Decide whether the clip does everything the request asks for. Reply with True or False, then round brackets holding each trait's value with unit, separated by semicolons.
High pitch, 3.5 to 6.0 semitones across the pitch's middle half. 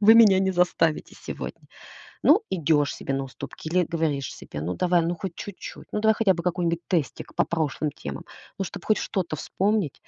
False (170 Hz; 3.9 semitones)